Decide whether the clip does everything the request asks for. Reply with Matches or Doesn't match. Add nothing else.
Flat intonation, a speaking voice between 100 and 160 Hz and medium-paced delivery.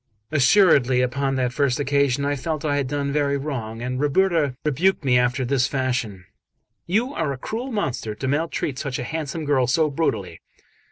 Doesn't match